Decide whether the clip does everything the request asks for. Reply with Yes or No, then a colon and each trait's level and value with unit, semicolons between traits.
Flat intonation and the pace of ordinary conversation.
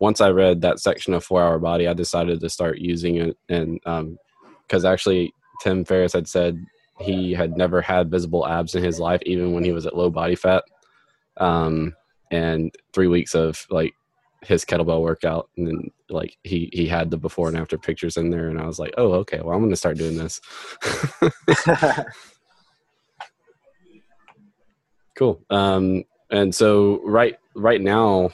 Yes: narrow, 1.7 semitones; average, 175 wpm